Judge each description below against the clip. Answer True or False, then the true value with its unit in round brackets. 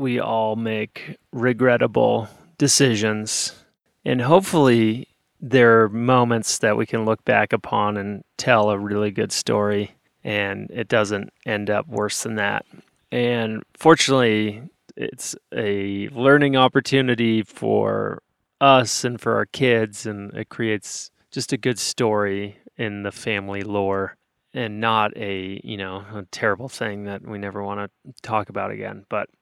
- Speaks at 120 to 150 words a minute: True (145 wpm)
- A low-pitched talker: True (110 Hz)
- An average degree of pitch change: True (3.3 semitones)